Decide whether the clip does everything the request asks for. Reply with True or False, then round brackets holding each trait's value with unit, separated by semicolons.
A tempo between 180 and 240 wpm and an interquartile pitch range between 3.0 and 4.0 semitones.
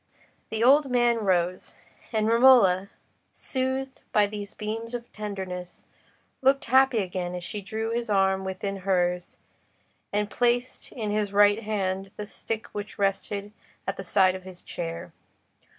False (145 wpm; 3.4 semitones)